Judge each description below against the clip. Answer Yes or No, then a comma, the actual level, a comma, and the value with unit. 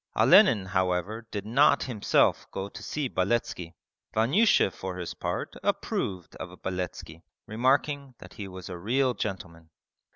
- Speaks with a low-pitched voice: Yes, low, 100 Hz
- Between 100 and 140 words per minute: Yes, slow, 135 wpm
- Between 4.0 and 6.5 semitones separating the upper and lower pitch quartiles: Yes, average, 5.1 semitones